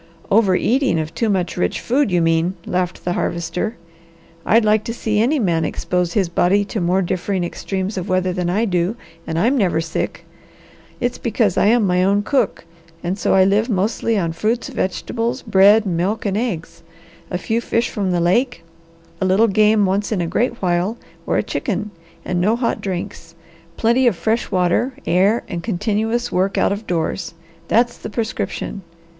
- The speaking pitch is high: Yes, high, 195 Hz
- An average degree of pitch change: Yes, average, 3.9 semitones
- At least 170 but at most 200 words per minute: Yes, average, 180 wpm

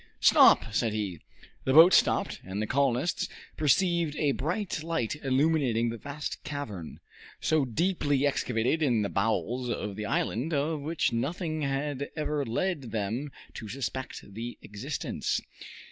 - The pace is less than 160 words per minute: Yes, average, 140 wpm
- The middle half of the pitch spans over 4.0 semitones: Yes, average, 5.0 semitones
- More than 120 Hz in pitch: Yes, low, 135 Hz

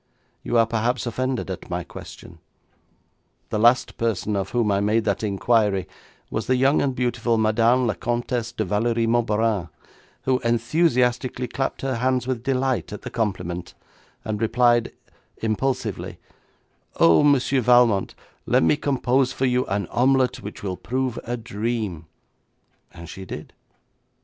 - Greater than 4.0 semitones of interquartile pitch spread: No, average, 3.1 semitones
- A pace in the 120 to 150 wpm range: Yes, average, 145 wpm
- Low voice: Yes, low, 115 Hz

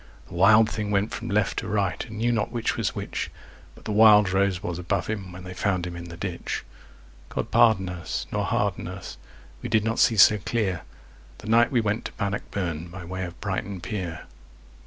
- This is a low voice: Yes, low, 100 Hz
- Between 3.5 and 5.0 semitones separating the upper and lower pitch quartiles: No, average, 3.1 semitones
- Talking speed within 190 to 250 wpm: Yes, fast, 205 wpm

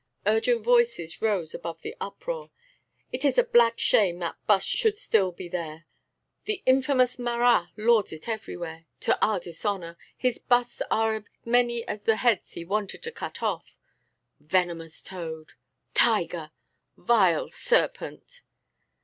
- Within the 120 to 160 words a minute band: Yes, average, 140 wpm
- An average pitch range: No, wide, 5.9 semitones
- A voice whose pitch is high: Yes, high, 215 Hz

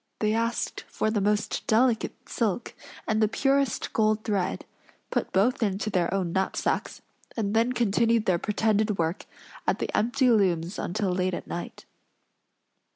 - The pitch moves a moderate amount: Yes, average, 3.1 semitones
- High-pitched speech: Yes, high, 215 Hz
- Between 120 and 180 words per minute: Yes, average, 150 wpm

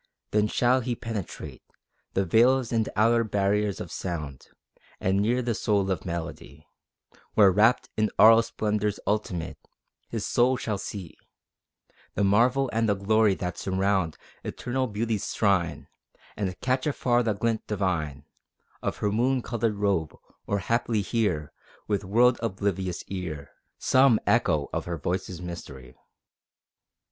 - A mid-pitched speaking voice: No, low, 105 Hz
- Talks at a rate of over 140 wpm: No, slow, 135 wpm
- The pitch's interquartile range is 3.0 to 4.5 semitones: Yes, average, 3.9 semitones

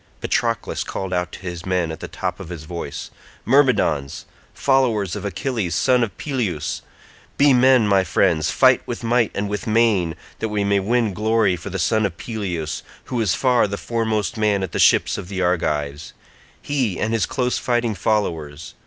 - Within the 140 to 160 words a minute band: No, average, 180 wpm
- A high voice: No, low, 105 Hz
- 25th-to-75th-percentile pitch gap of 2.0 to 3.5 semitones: No, average, 4.9 semitones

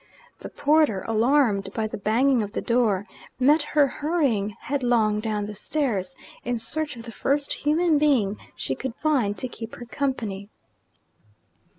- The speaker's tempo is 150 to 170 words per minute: Yes, average, 155 wpm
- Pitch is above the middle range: Yes, high, 240 Hz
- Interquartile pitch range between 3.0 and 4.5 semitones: No, wide, 5.4 semitones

